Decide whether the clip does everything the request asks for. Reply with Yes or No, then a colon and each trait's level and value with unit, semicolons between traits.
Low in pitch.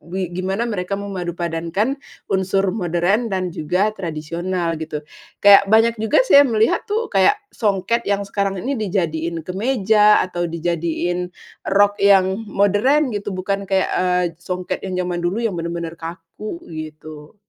No: high, 190 Hz